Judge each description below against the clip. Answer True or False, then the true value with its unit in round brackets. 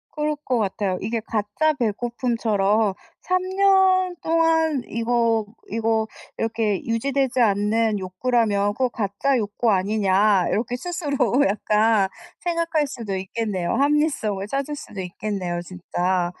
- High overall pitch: True (225 Hz)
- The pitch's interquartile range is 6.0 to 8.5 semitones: False (5.4 semitones)